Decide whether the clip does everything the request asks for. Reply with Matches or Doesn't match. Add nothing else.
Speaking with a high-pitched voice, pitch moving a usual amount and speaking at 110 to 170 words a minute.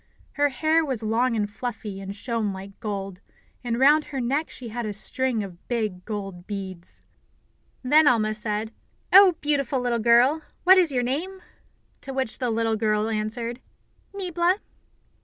Matches